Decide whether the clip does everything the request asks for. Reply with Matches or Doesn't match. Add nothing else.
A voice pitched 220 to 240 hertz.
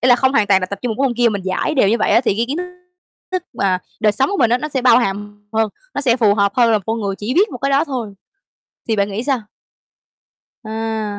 Matches